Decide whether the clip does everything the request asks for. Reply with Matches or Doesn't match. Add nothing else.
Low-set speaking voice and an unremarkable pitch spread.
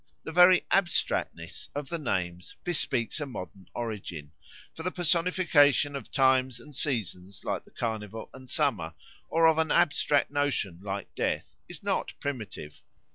Doesn't match